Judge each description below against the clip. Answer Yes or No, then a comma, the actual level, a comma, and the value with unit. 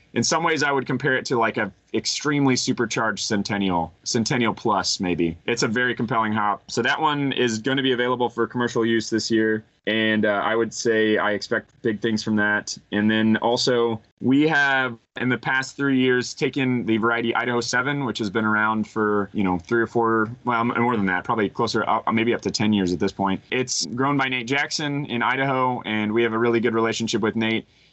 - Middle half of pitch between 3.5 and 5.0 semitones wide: No, narrow, 2.6 semitones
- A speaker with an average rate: No, fast, 215 wpm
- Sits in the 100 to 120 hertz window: Yes, low, 115 Hz